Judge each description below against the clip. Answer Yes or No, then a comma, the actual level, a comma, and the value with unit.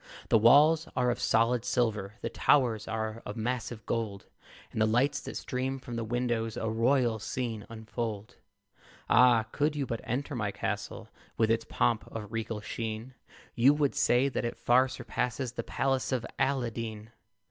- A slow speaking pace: No, average, 165 wpm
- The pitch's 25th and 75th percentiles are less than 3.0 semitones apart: Yes, narrow, 2.5 semitones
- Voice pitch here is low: Yes, low, 115 Hz